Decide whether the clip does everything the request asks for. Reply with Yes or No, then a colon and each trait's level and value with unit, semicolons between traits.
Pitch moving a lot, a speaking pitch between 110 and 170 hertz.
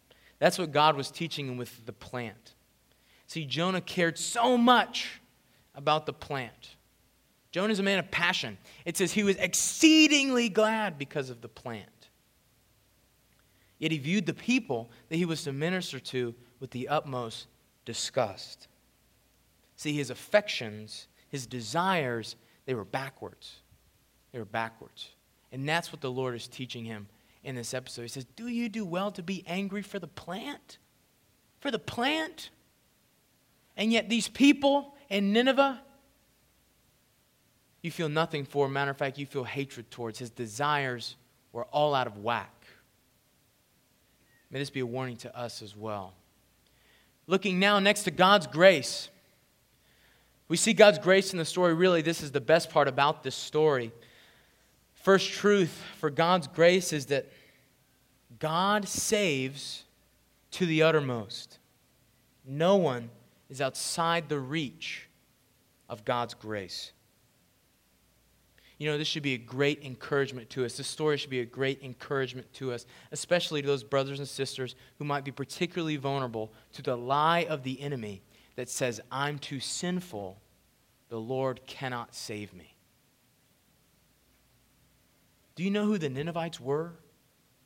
Yes: wide, 5.9 semitones; medium, 140 Hz